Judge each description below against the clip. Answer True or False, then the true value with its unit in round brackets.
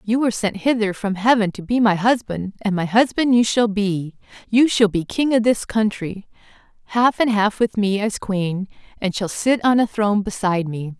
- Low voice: False (210 Hz)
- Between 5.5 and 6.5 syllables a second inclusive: False (4.9 syllables/s)